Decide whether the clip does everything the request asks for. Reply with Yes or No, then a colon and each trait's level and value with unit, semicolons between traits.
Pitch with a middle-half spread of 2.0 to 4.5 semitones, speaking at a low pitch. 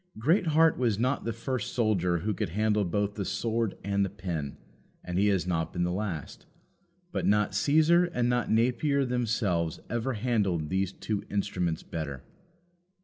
No: average, 5.0 semitones; low, 105 Hz